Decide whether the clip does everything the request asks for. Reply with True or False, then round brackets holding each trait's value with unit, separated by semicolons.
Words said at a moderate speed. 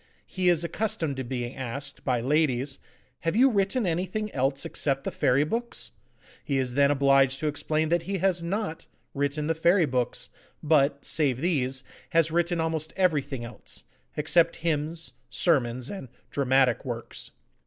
True (155 wpm)